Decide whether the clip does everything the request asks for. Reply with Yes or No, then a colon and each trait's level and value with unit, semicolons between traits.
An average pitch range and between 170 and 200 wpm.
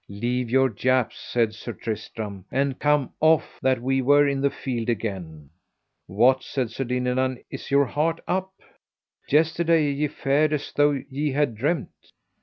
No: average, 3.5 semitones; average, 155 wpm